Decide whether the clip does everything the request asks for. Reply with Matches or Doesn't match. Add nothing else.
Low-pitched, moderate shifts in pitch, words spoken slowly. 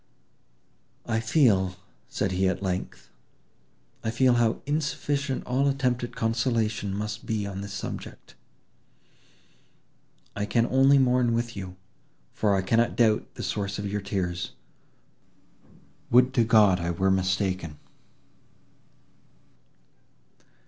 Matches